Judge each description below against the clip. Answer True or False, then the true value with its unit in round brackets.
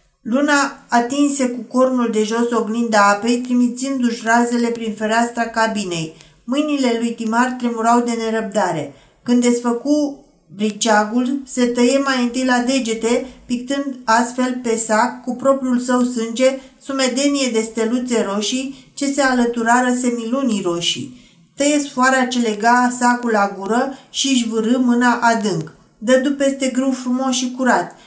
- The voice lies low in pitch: False (245 Hz)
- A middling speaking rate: True (135 wpm)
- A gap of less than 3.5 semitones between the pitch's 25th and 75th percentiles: True (2.4 semitones)